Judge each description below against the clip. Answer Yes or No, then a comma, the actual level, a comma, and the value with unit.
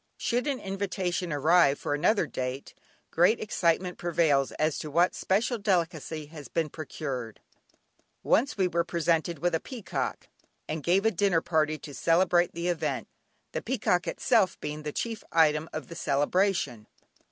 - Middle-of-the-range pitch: Yes, medium, 170 Hz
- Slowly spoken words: No, average, 150 wpm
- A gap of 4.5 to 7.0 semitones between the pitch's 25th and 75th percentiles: No, average, 3.7 semitones